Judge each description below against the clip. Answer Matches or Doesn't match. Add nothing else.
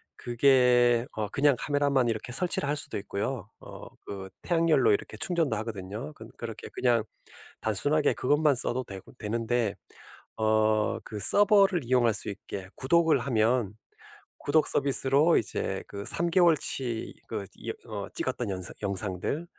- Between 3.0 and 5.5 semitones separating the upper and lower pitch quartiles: Matches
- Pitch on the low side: Matches